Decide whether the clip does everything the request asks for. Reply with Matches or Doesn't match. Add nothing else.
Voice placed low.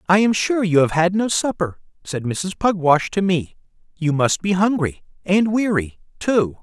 Doesn't match